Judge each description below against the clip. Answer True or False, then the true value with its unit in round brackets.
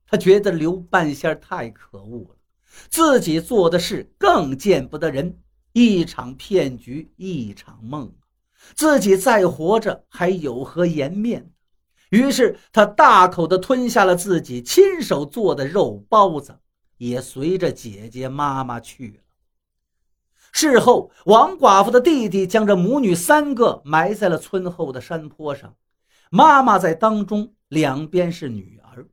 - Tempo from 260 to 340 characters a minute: False (200 characters per minute)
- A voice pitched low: False (165 Hz)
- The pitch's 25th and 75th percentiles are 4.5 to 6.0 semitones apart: False (7.6 semitones)